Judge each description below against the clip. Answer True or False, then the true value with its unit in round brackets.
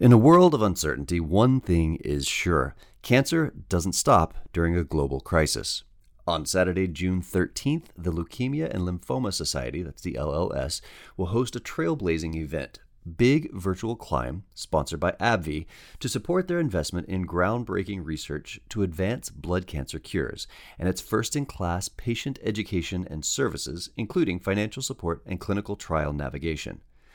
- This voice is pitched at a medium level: False (90 Hz)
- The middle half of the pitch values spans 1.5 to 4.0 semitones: False (5.3 semitones)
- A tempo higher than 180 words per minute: False (145 wpm)